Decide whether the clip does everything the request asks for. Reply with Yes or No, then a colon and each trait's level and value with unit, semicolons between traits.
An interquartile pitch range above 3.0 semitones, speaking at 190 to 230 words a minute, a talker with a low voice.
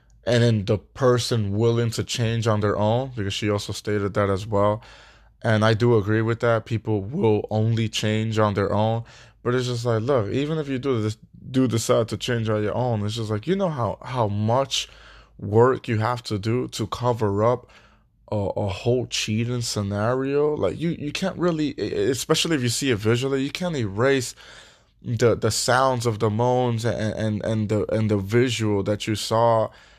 No: narrow, 2.5 semitones; average, 195 wpm; low, 115 Hz